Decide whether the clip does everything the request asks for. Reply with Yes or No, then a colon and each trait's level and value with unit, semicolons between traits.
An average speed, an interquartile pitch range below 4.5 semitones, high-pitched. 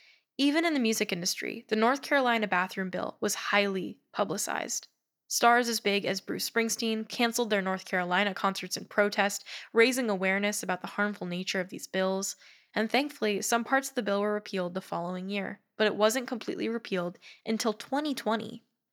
Yes: average, 170 wpm; average, 3.4 semitones; high, 210 Hz